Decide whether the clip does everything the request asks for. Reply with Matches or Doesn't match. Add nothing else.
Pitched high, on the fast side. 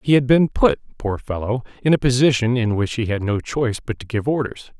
Doesn't match